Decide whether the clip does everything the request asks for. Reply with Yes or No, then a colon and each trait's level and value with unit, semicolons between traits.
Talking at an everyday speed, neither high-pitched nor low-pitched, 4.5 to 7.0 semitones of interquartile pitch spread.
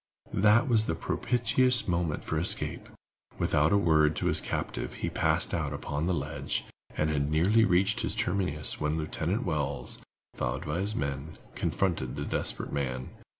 No: average, 160 wpm; very low, 80 Hz; average, 5.1 semitones